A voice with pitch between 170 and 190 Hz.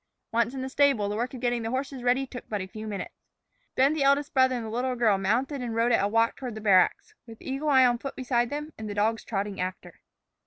No: high, 240 Hz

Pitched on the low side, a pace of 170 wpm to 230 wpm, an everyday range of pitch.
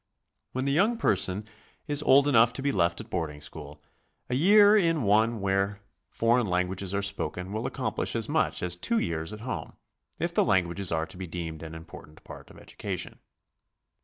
No: low, 100 Hz; average, 190 wpm; wide, 6.8 semitones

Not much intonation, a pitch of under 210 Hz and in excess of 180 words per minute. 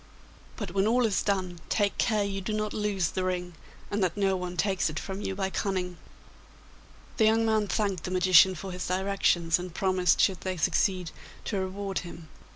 Yes: narrow, 2.1 semitones; high, 190 Hz; average, 190 wpm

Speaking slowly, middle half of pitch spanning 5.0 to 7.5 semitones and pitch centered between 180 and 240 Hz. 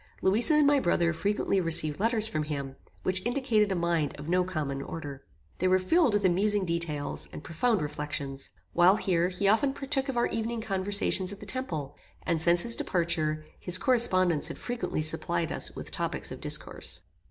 No: average, 180 wpm; wide, 5.6 semitones; medium, 185 Hz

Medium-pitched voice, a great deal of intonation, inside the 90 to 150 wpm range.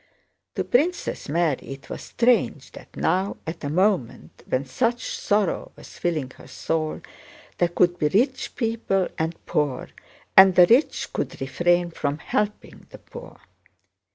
Yes: medium, 175 Hz; wide, 5.8 semitones; average, 145 wpm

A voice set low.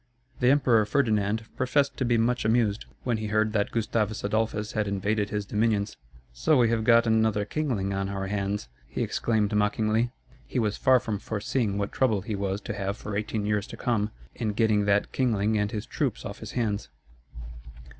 Yes: low, 110 Hz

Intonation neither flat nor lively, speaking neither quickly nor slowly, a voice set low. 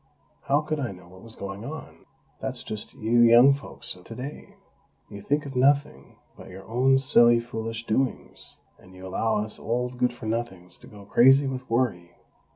Yes: average, 4.3 semitones; average, 185 wpm; low, 120 Hz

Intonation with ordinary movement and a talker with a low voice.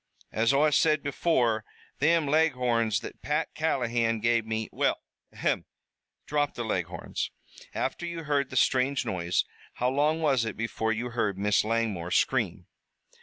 Yes: average, 4.7 semitones; low, 120 Hz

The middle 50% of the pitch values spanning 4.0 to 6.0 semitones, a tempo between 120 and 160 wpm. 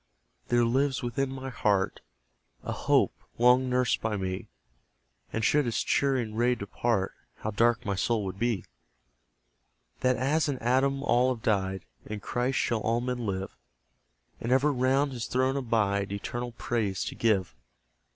No: average, 3.5 semitones; average, 150 wpm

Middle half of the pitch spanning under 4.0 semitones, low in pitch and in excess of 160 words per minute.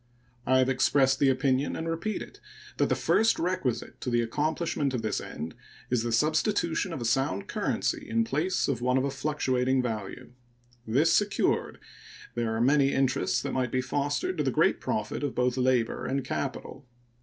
Yes: average, 3.0 semitones; low, 130 Hz; average, 180 wpm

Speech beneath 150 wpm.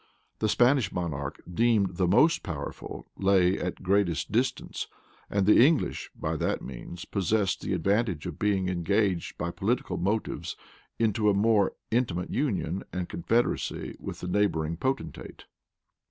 Yes: average, 140 wpm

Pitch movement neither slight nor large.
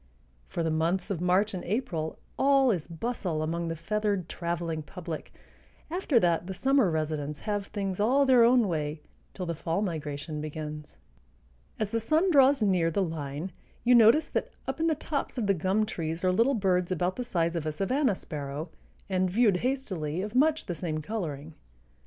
No: wide, 6.0 semitones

